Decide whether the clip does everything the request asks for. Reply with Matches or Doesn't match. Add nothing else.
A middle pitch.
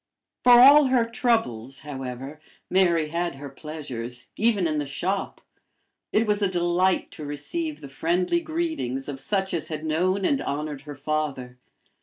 Matches